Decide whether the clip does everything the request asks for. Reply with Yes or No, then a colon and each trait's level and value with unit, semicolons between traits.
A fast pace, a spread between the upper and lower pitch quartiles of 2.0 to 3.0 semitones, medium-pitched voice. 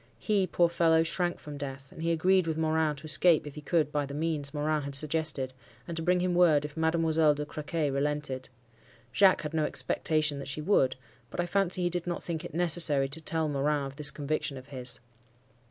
Yes: fast, 215 wpm; narrow, 2.6 semitones; medium, 155 Hz